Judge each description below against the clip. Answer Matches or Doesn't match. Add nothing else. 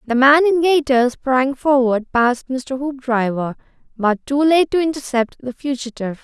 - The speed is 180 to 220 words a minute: Doesn't match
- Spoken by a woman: Matches